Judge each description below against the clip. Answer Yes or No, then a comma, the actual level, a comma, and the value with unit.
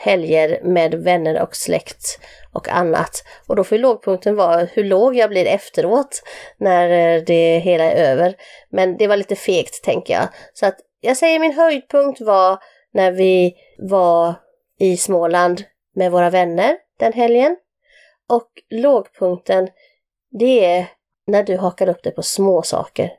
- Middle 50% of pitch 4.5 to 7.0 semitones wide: Yes, average, 5.3 semitones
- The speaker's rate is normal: Yes, average, 150 wpm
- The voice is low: No, high, 190 Hz